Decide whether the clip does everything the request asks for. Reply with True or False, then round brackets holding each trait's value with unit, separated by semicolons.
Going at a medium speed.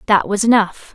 True (190 wpm)